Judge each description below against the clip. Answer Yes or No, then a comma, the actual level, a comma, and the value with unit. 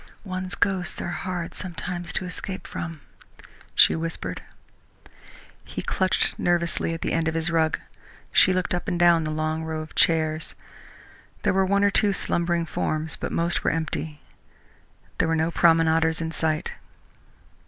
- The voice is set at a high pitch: No, medium, 165 Hz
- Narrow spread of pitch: Yes, narrow, 1.8 semitones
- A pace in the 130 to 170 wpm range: Yes, average, 155 wpm